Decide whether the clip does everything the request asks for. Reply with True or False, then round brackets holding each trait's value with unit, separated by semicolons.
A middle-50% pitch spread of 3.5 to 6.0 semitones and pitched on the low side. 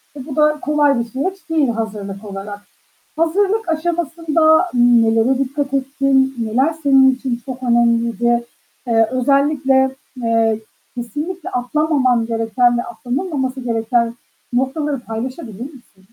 False (4.2 semitones; 260 Hz)